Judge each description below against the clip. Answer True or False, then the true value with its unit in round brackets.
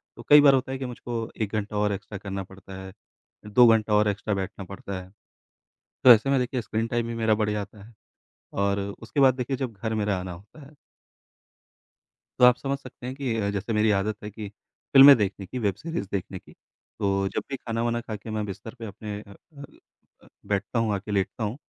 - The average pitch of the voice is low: True (110 Hz)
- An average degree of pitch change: True (3.4 semitones)